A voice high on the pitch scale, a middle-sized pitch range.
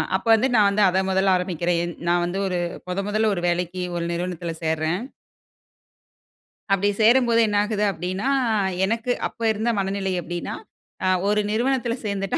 Yes: high, 195 Hz; average, 3.4 semitones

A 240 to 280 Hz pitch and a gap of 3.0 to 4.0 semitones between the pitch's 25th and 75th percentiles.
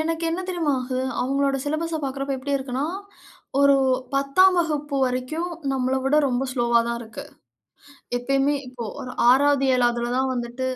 No: very high, 270 Hz; narrow, 2.5 semitones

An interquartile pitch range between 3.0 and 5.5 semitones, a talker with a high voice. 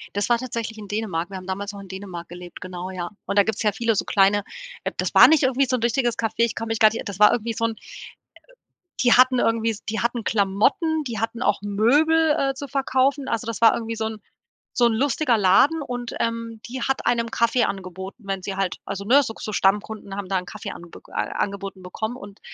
Yes: average, 3.5 semitones; high, 220 Hz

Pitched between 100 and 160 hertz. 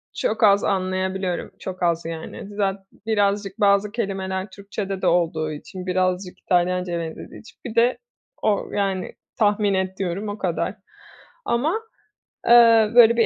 No: high, 195 Hz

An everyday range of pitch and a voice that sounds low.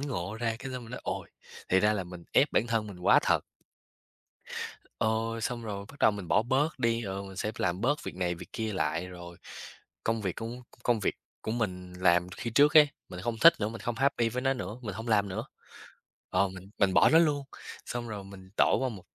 Yes: average, 4.3 semitones; low, 110 Hz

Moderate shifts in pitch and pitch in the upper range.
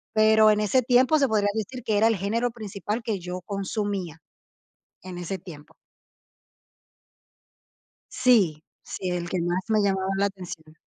Yes: average, 3.4 semitones; high, 200 Hz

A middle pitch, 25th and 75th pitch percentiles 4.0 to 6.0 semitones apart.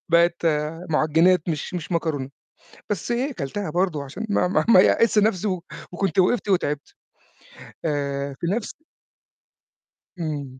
Yes: medium, 170 Hz; average, 4.6 semitones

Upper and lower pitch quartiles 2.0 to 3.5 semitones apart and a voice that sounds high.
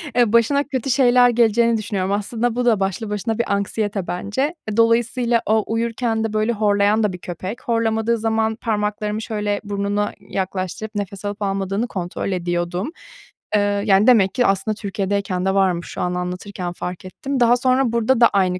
Yes: average, 2.9 semitones; high, 210 Hz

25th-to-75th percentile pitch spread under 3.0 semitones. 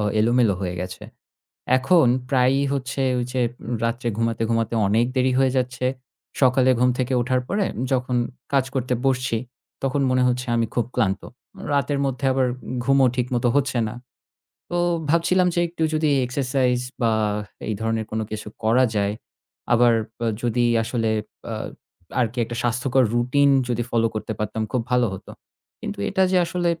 Yes: narrow, 2.6 semitones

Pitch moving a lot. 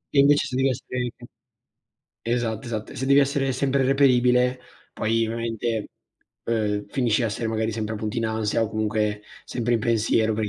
No: narrow, 2.6 semitones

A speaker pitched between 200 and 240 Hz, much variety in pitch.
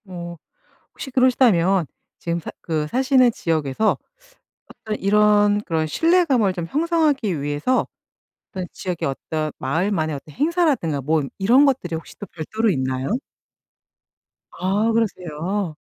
No: high, 190 Hz; wide, 7.2 semitones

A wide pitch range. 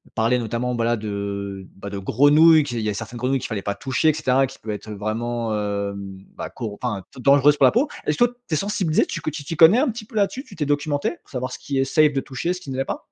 Yes: wide, 6.0 semitones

